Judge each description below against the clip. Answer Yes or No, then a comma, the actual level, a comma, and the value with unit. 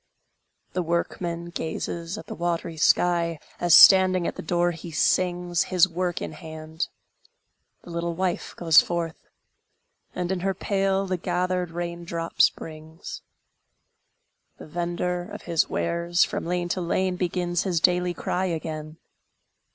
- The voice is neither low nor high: Yes, medium, 175 Hz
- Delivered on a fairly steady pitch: Yes, narrow, 1.3 semitones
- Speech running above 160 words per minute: No, average, 140 wpm